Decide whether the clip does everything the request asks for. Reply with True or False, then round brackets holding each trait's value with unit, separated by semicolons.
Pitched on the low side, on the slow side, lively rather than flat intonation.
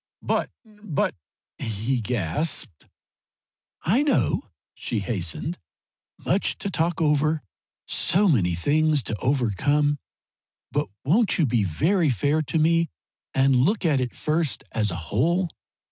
False (145 Hz; 130 wpm; 6.5 semitones)